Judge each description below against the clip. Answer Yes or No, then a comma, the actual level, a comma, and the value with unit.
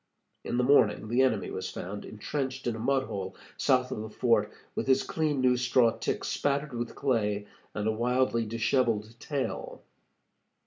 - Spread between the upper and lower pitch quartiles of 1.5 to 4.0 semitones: Yes, average, 3.2 semitones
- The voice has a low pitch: Yes, low, 120 Hz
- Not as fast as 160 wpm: No, average, 170 wpm